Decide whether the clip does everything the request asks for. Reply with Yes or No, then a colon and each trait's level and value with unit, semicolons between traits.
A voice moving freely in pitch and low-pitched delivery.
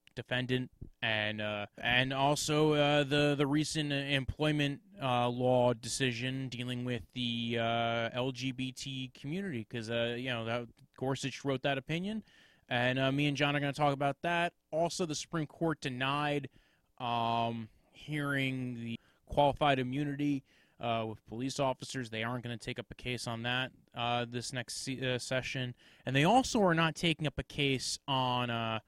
No: average, 3.3 semitones; low, 130 Hz